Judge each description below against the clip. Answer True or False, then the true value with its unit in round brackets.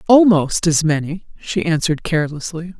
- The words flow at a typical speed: False (130 wpm)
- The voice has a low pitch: False (170 Hz)